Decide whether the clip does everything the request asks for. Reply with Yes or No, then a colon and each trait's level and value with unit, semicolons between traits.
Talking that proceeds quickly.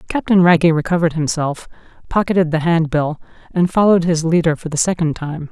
No: average, 165 wpm